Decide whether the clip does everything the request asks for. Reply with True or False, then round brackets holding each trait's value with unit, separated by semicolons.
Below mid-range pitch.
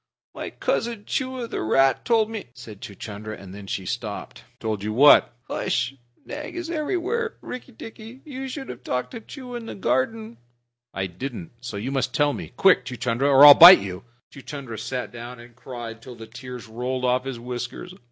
True (130 Hz)